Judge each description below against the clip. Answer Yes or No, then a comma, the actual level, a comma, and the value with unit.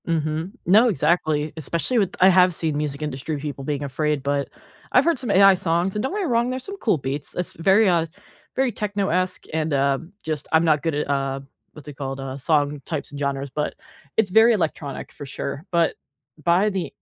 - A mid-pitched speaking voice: Yes, medium, 160 Hz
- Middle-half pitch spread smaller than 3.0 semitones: No, average, 5.0 semitones